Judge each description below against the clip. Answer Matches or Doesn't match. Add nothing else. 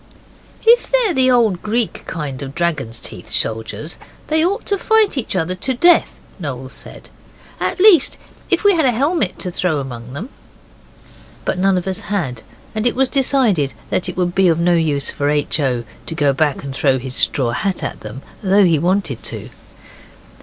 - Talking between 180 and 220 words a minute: Matches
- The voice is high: Doesn't match